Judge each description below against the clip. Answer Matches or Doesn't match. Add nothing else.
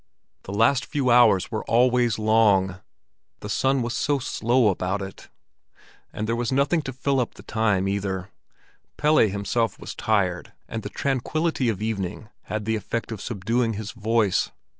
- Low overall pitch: Matches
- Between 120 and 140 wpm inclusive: Doesn't match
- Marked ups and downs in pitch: Doesn't match